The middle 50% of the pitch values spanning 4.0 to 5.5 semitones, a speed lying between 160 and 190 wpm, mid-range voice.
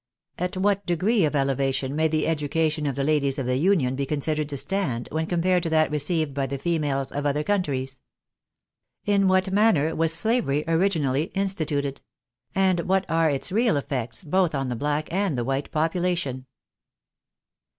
Yes: average, 4.6 semitones; average, 180 wpm; medium, 155 Hz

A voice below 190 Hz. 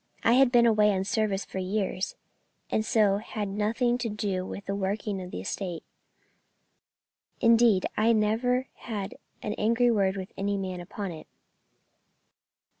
No: high, 210 Hz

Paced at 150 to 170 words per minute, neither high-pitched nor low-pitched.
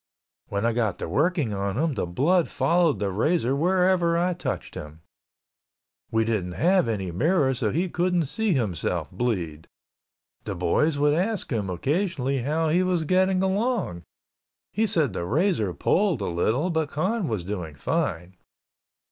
Yes: average, 155 wpm; medium, 145 Hz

